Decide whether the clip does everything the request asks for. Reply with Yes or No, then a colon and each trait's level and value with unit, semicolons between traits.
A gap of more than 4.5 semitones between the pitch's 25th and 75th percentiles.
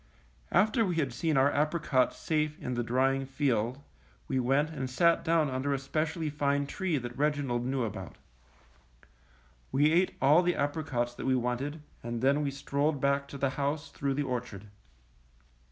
No: average, 2.8 semitones